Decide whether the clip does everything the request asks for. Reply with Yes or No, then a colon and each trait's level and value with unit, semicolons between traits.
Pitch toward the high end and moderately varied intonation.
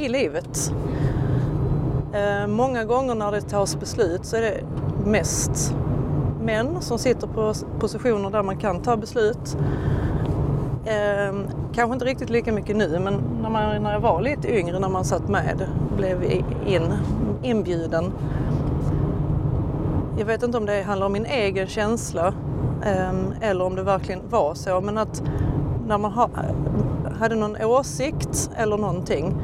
No: high, 200 Hz; wide, 7.2 semitones